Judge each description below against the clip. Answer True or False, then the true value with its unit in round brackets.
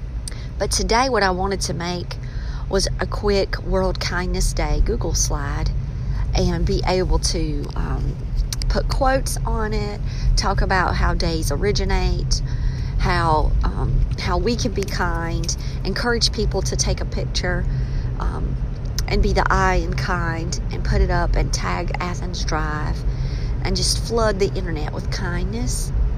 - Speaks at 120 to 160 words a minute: True (145 wpm)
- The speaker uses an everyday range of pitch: False (7.1 semitones)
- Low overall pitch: False (185 Hz)